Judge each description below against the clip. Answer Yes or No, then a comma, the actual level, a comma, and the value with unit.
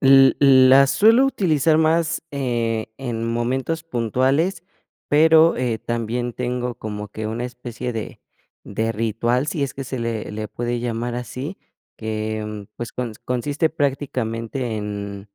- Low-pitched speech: Yes, low, 125 Hz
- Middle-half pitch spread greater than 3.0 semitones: Yes, average, 3.5 semitones